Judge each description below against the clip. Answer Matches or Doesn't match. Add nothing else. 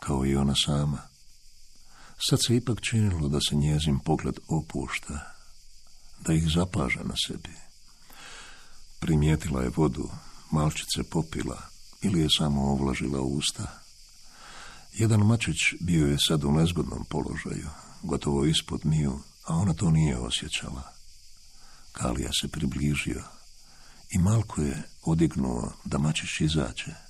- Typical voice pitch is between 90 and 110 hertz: Doesn't match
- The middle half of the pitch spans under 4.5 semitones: Matches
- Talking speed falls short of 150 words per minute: Matches